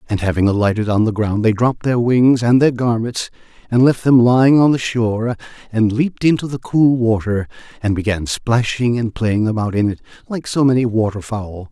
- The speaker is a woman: No, male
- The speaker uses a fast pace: No, average, 195 wpm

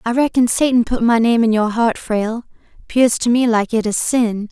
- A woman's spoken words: Yes, female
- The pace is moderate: No, fast, 225 wpm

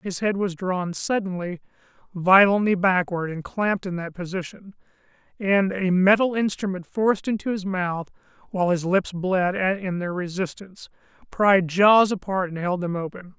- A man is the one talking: Yes, male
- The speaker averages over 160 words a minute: No, average, 150 wpm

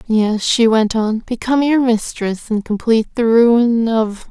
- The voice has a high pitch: Yes, high, 225 Hz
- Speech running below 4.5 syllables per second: Yes, 4.1 syllables/s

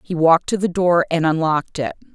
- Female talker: Yes, female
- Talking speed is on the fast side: Yes, fast, 225 wpm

